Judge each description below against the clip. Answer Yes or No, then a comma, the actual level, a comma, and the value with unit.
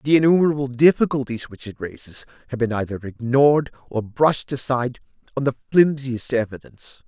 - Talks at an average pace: Yes, average, 145 wpm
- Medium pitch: No, low, 130 Hz